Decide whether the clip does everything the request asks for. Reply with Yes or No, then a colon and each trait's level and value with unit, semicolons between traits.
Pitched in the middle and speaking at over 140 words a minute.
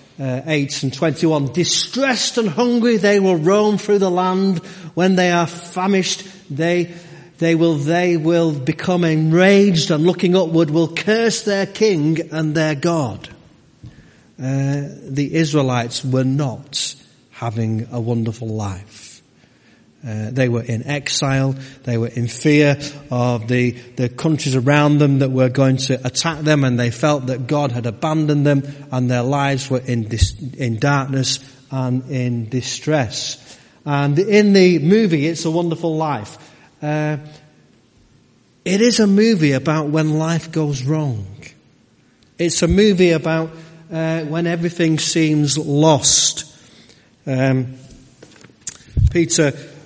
No: medium, 150 Hz; slow, 135 wpm